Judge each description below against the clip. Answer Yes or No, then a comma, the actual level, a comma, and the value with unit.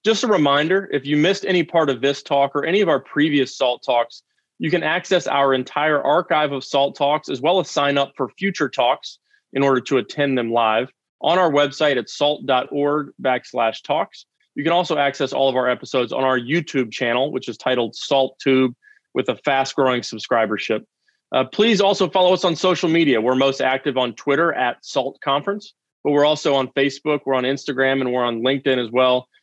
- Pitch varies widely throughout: No, average, 2.7 semitones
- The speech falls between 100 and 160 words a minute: No, fast, 205 wpm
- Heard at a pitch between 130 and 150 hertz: Yes, medium, 140 Hz